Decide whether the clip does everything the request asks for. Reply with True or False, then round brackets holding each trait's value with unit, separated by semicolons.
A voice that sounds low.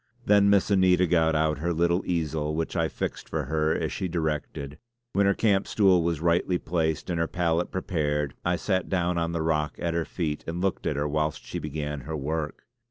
True (85 Hz)